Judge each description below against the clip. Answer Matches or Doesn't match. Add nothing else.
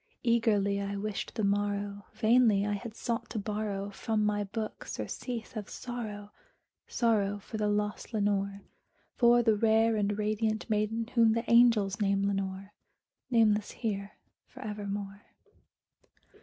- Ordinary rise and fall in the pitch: Doesn't match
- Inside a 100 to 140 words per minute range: Matches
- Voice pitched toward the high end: Matches